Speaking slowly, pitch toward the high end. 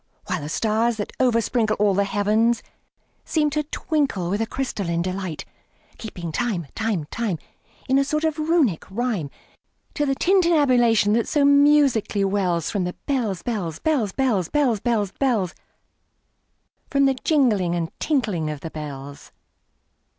Yes: slow, 125 wpm; high, 220 Hz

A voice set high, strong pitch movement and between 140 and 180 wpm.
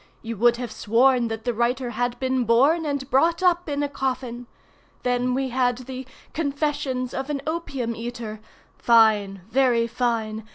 No: very high, 250 Hz; narrow, 2.5 semitones; average, 155 wpm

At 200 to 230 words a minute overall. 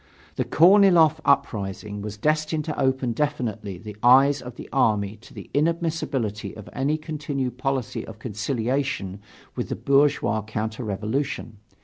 No: slow, 135 wpm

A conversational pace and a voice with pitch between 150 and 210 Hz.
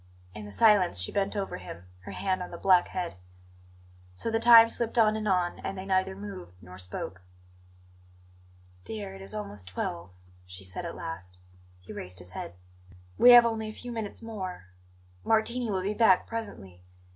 Yes: average, 180 wpm; medium, 185 Hz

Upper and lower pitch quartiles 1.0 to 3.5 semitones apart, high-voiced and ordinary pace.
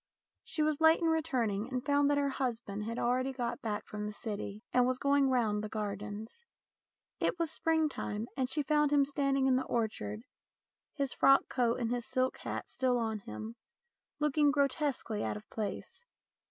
No: average, 4.6 semitones; very high, 255 Hz; average, 180 wpm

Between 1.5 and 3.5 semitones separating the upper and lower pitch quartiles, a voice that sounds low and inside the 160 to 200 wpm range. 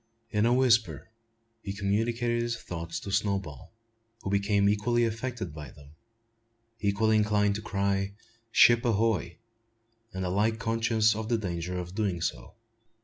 No: average, 3.1 semitones; low, 105 Hz; average, 140 wpm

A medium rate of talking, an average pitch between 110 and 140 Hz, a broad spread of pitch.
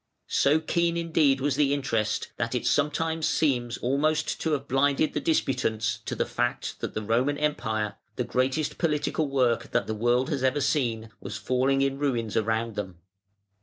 No: average, 170 wpm; low, 135 Hz; average, 4.3 semitones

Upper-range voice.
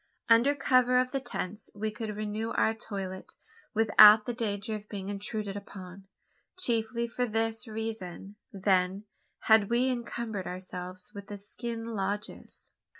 Yes: high, 215 Hz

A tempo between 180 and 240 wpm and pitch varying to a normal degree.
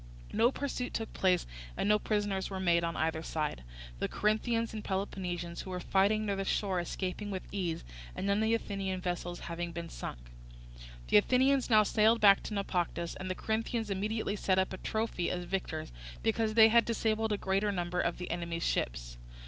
Yes: average, 190 wpm; average, 3.6 semitones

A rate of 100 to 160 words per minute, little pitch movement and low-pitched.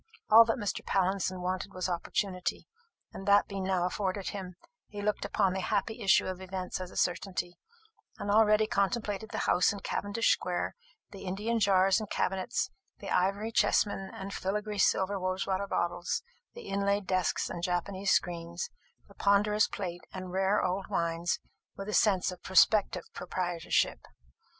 No: average, 155 wpm; narrow, 1.9 semitones; high, 195 Hz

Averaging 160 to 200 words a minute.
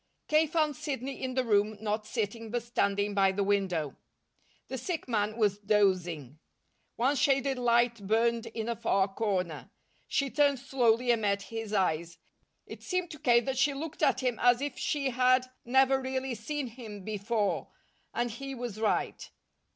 Yes: average, 165 wpm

